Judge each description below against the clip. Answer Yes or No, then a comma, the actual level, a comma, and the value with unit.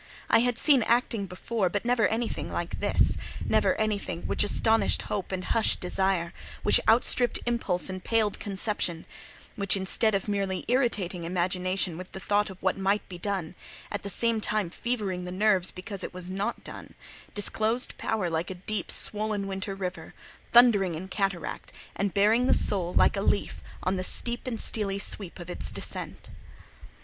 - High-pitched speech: Yes, high, 200 Hz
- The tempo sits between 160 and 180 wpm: Yes, average, 170 wpm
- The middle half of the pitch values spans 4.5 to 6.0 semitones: No, average, 2.9 semitones